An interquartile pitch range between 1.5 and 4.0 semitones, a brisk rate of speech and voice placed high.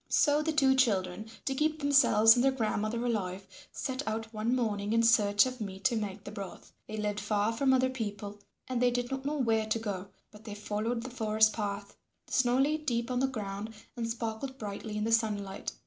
Yes: average, 3.6 semitones; fast, 210 wpm; high, 225 Hz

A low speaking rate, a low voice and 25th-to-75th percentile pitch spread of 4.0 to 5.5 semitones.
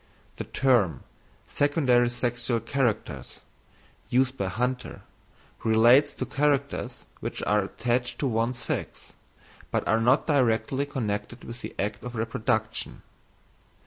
No: slow, 115 wpm; low, 120 Hz; average, 2.9 semitones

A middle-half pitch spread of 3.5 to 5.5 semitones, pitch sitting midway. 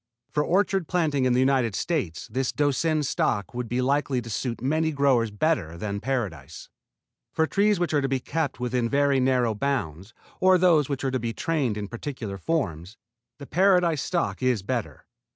No: average, 5.1 semitones; low, 130 Hz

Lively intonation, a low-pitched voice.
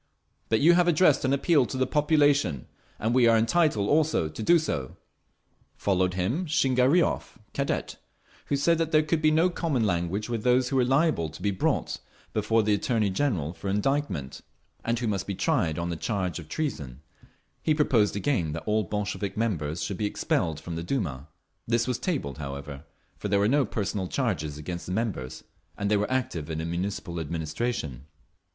Yes: wide, 8.1 semitones; low, 105 Hz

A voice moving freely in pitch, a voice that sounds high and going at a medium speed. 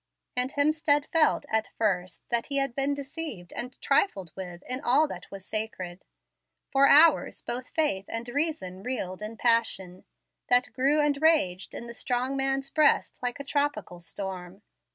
Yes: wide, 6.6 semitones; very high, 250 Hz; average, 160 wpm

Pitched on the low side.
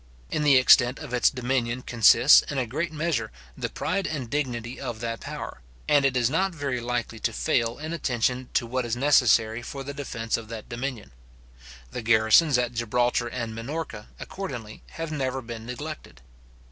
Yes: low, 125 Hz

